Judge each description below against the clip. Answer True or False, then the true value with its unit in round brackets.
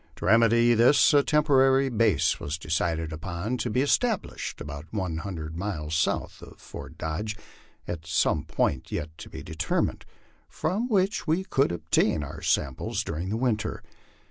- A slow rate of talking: False (155 wpm)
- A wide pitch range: True (8.5 semitones)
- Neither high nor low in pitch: False (100 Hz)